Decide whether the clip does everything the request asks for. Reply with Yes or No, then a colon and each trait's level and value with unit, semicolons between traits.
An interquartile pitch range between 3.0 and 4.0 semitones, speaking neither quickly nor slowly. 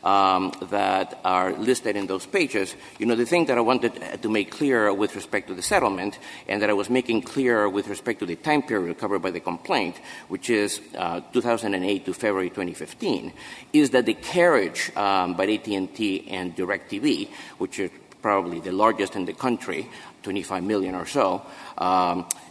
No: average, 4.9 semitones; average, 180 wpm